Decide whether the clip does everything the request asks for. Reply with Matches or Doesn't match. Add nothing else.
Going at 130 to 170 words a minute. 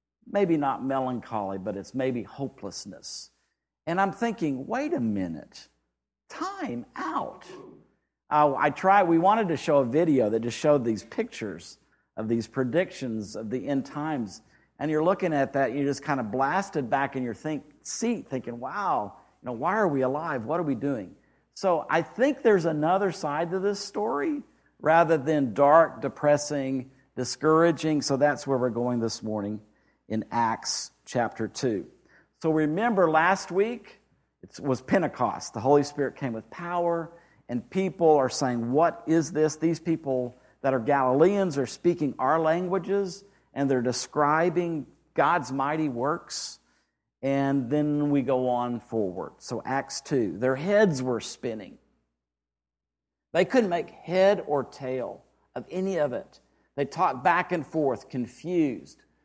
Matches